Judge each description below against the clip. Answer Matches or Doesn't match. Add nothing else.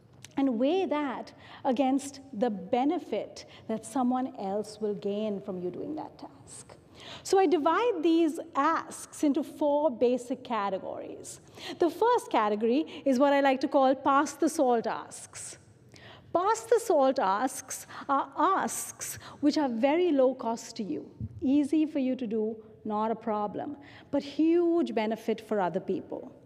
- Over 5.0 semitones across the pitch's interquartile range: Matches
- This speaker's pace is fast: Doesn't match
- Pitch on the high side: Matches